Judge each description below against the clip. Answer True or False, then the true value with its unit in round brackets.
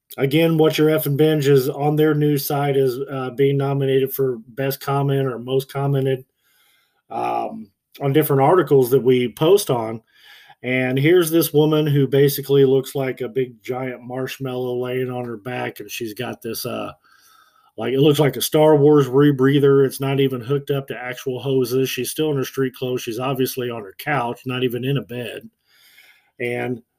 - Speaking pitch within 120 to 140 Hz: True (135 Hz)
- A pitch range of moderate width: False (2.0 semitones)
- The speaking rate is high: False (180 wpm)